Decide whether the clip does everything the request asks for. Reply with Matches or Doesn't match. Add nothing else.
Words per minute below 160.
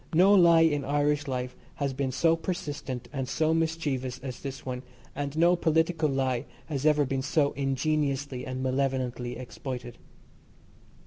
Matches